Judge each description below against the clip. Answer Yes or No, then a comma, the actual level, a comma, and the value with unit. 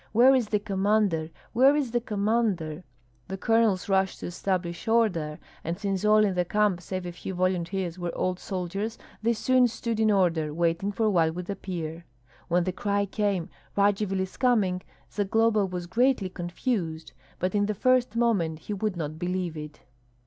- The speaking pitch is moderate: No, high, 195 Hz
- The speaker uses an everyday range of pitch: Yes, average, 3.6 semitones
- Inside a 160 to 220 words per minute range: Yes, average, 170 wpm